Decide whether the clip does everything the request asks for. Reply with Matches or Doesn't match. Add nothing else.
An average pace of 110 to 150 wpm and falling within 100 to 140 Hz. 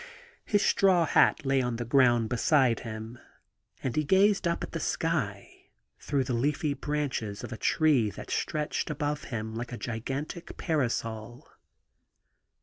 Matches